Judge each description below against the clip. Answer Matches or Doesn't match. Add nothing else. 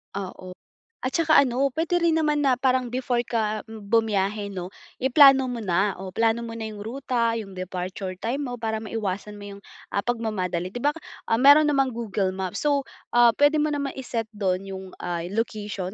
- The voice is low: Doesn't match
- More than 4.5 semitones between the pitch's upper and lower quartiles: Matches